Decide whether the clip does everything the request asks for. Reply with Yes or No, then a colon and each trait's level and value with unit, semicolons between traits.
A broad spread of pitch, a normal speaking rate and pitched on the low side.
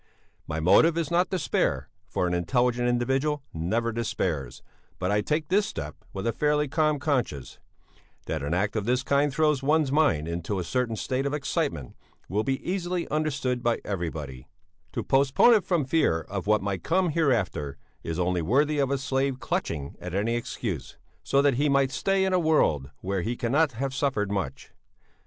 Yes: wide, 7.9 semitones; average, 180 wpm; low, 125 Hz